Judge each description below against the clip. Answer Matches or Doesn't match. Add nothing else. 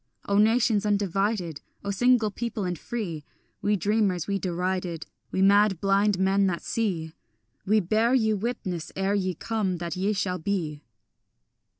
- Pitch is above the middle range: Matches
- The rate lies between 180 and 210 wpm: Doesn't match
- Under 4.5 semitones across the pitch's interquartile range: Matches